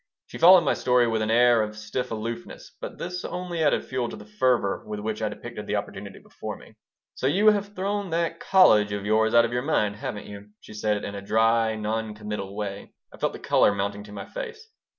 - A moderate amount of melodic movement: No, wide, 6.9 semitones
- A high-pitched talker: No, low, 110 Hz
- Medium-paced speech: No, fast, 225 wpm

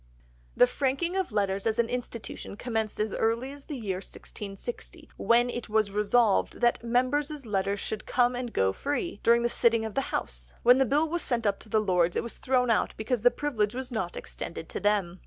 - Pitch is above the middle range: Yes, high, 230 Hz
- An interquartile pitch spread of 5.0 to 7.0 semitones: No, average, 3.5 semitones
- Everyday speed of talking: No, fast, 210 wpm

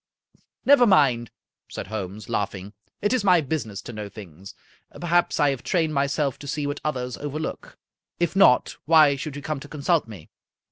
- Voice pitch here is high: No, medium, 140 Hz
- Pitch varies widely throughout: Yes, wide, 6.1 semitones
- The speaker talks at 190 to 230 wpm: Yes, average, 195 wpm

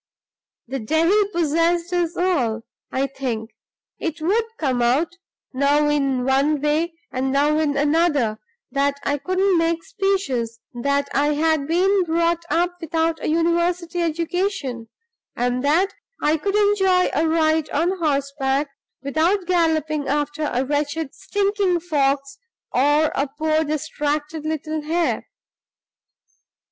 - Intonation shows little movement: No, average, 3.4 semitones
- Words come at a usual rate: No, slow, 125 wpm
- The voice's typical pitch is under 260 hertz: No, very high, 310 Hz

